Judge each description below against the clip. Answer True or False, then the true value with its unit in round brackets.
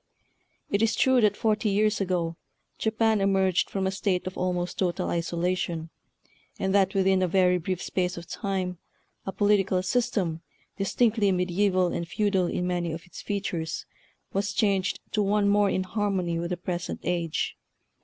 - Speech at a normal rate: True (160 wpm)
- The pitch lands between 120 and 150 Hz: False (190 Hz)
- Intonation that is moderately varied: False (2.3 semitones)